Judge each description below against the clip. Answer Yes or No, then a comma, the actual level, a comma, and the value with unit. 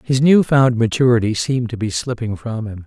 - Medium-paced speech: No, fast, 210 wpm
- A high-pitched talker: No, low, 120 Hz